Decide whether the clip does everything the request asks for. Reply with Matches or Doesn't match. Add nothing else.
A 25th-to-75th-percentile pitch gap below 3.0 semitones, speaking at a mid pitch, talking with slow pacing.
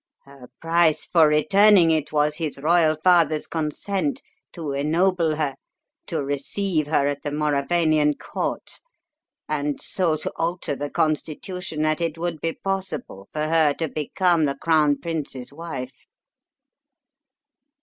Matches